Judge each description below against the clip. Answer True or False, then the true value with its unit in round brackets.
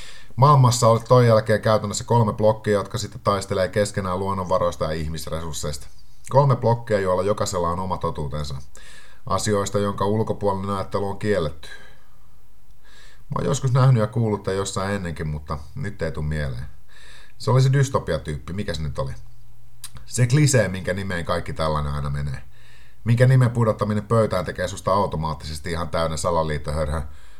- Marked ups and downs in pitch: True (6.3 semitones)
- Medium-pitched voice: False (100 Hz)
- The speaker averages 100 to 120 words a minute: False (145 wpm)